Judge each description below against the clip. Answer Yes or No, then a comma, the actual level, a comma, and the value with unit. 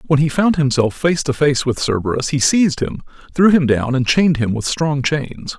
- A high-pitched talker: No, medium, 140 Hz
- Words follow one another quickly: Yes, fast, 225 wpm